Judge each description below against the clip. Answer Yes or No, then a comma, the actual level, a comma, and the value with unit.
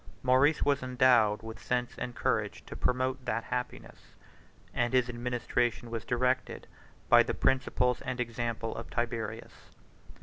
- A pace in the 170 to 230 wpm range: No, slow, 135 wpm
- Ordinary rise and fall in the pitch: No, narrow, 1.6 semitones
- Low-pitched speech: Yes, low, 125 Hz